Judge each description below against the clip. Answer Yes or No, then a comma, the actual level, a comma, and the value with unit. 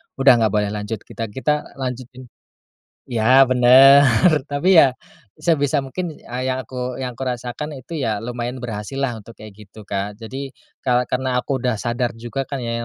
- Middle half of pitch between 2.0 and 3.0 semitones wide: Yes, average, 2.7 semitones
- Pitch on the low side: Yes, low, 125 Hz